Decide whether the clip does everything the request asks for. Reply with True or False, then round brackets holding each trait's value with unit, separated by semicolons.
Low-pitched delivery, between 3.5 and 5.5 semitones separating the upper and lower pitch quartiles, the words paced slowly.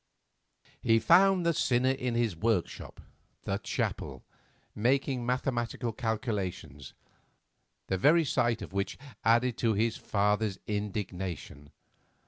True (115 Hz; 4.1 semitones; 110 wpm)